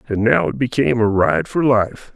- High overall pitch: No, low, 115 Hz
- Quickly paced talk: Yes, fast, 225 wpm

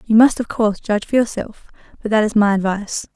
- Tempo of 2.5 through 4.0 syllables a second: No, 6.4 syllables/s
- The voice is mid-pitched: No, high, 215 Hz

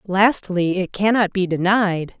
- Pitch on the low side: No, high, 195 Hz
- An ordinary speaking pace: Yes, average, 165 wpm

